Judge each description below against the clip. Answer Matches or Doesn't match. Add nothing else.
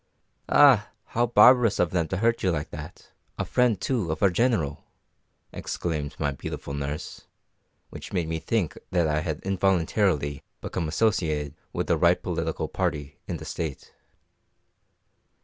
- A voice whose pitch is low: Matches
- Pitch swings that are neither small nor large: Doesn't match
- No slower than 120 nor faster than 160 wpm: Matches